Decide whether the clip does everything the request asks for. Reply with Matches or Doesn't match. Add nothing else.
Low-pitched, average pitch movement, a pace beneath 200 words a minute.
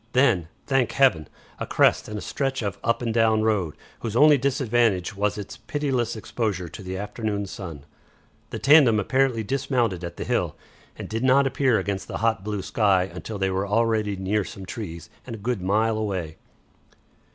Matches